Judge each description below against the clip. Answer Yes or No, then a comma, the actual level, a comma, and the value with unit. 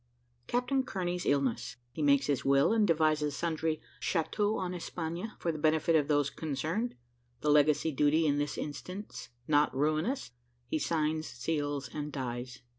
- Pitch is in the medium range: Yes, medium, 155 Hz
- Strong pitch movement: No, average, 2.7 semitones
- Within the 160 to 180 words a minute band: No, average, 150 wpm